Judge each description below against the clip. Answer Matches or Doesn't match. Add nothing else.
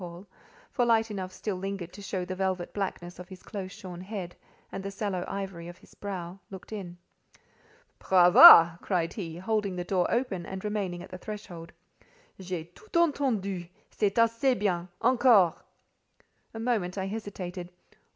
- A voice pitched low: Doesn't match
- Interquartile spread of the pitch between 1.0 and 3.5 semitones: Matches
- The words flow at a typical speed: Matches